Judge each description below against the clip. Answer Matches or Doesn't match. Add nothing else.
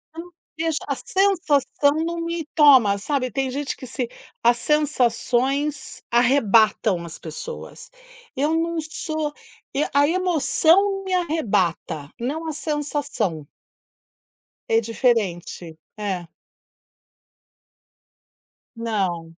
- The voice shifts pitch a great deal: Matches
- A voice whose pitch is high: Matches